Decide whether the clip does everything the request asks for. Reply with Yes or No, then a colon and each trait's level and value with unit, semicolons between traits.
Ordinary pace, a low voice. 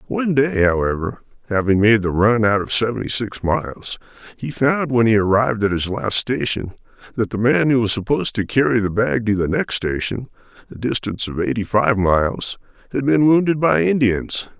Yes: average, 190 wpm; low, 115 Hz